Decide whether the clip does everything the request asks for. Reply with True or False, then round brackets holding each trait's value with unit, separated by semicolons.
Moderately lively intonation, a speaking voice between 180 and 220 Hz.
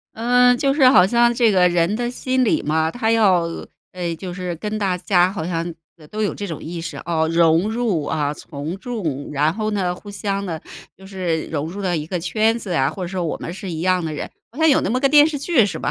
True (5.0 semitones; 185 Hz)